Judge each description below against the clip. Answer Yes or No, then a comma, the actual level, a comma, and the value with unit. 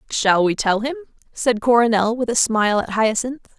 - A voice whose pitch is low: No, high, 230 Hz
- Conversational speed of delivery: Yes, average, 185 wpm